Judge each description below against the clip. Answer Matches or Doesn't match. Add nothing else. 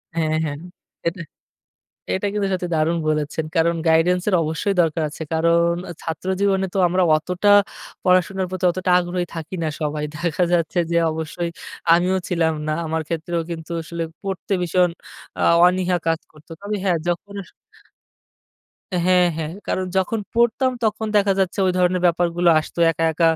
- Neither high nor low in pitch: Matches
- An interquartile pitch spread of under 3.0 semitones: Matches